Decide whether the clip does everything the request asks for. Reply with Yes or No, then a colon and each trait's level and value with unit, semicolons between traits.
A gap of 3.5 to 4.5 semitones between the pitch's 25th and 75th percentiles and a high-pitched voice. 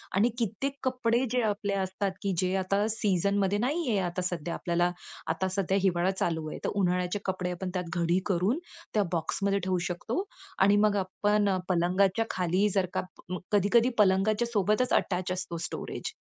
No: narrow, 2.5 semitones; high, 195 Hz